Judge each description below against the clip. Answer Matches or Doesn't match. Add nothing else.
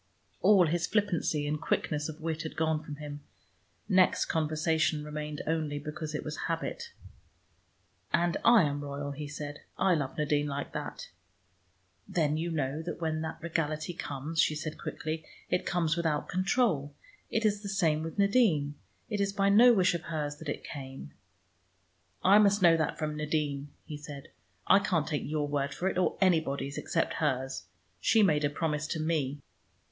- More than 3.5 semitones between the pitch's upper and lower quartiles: Doesn't match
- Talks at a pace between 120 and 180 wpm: Matches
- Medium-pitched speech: Matches